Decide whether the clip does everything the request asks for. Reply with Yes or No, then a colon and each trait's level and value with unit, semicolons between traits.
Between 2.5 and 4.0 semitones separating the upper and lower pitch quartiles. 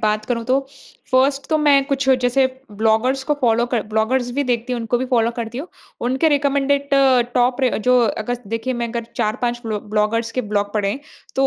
Yes: average, 3.0 semitones